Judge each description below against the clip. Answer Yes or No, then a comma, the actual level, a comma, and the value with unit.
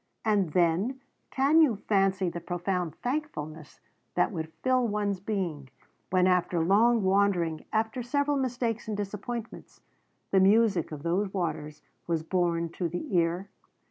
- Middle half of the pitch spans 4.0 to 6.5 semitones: Yes, average, 4.7 semitones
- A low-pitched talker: No, high, 190 Hz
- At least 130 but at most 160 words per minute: Yes, average, 140 wpm